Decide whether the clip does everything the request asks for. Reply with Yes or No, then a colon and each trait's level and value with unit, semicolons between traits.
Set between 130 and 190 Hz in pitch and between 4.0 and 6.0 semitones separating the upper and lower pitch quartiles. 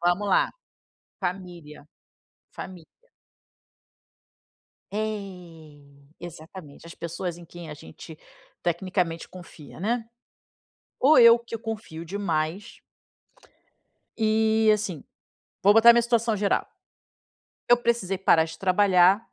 Yes: medium, 185 Hz; average, 4.4 semitones